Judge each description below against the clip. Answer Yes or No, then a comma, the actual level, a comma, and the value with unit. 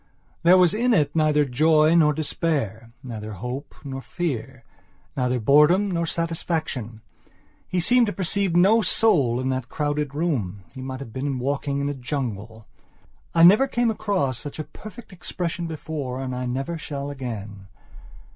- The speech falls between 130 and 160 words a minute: Yes, average, 155 wpm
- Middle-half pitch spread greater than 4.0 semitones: Yes, average, 4.9 semitones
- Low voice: No, medium, 145 Hz